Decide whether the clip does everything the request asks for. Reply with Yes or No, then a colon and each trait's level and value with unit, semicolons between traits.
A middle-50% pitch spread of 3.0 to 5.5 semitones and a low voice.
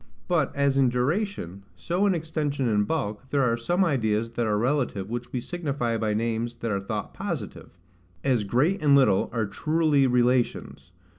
Yes: average, 4.8 semitones; low, 125 Hz